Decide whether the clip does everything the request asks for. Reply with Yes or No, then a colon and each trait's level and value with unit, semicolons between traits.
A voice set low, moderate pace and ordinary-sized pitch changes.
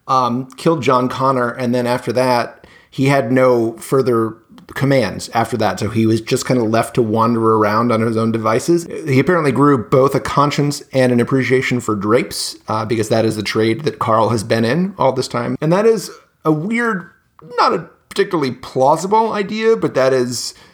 Yes: low, 130 Hz; average, 195 wpm; average, 4.1 semitones